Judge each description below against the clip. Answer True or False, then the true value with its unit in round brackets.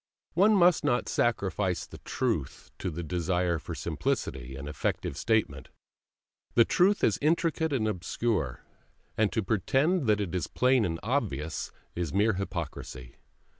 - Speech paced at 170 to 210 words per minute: False (140 wpm)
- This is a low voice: True (105 Hz)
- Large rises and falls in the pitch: True (7.1 semitones)